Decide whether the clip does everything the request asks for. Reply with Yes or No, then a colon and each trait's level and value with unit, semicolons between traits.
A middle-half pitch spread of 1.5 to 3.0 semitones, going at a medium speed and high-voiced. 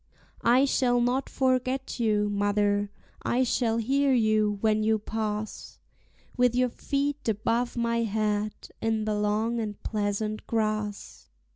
No: average, 2.7 semitones; slow, 130 wpm; high, 220 Hz